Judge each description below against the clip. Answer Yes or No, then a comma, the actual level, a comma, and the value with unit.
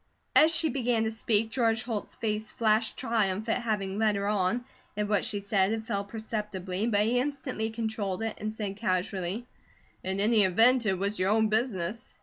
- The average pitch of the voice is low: No, high, 215 Hz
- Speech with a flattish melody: Yes, narrow, 2.3 semitones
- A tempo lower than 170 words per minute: No, average, 185 wpm